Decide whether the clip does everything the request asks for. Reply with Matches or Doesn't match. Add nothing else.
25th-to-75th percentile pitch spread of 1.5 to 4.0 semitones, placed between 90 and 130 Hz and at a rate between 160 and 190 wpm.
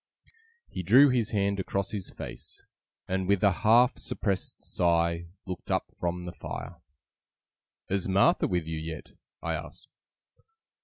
Doesn't match